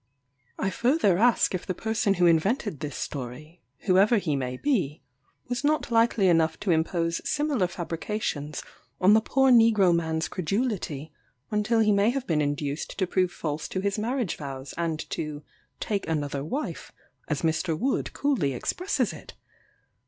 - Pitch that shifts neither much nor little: No, wide, 6.1 semitones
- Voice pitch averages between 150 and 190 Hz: Yes, medium, 185 Hz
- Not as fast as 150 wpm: No, average, 155 wpm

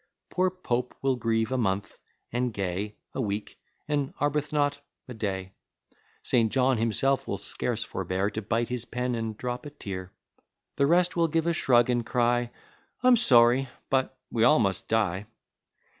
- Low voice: Yes, low, 120 Hz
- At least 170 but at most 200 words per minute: No, average, 160 wpm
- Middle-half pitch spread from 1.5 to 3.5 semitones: No, average, 3.9 semitones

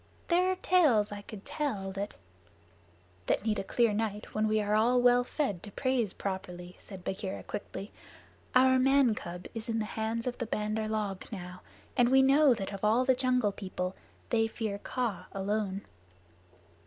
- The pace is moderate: Yes, average, 180 wpm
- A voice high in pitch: Yes, high, 215 Hz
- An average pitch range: Yes, average, 4.1 semitones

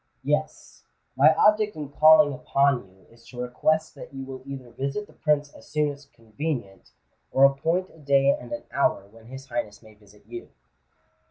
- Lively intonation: No, average, 3.8 semitones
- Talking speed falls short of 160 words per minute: No, average, 180 wpm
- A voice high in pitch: No, medium, 140 Hz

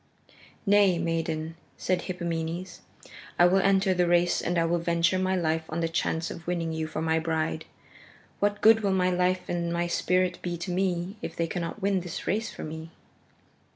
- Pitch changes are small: Yes, narrow, 2.0 semitones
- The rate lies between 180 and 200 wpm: Yes, average, 190 wpm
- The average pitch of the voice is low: No, medium, 175 Hz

